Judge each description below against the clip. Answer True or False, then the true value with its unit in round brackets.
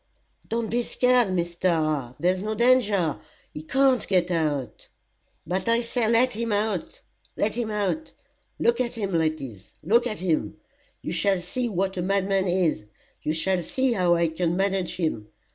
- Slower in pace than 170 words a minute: True (160 wpm)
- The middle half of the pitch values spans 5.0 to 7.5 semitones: True (5.4 semitones)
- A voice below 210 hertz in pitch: True (190 Hz)